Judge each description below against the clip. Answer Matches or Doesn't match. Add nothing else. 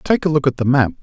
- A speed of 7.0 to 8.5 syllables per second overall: Doesn't match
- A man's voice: Matches